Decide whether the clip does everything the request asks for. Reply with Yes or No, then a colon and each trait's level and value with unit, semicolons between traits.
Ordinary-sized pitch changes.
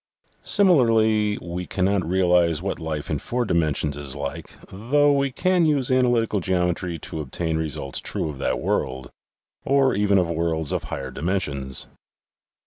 No: wide, 6.3 semitones